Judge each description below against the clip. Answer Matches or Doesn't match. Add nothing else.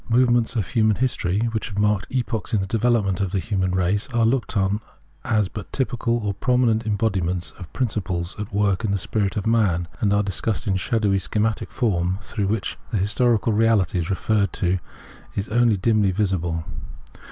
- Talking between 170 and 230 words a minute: Matches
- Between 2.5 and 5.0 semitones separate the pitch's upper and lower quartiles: Matches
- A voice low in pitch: Matches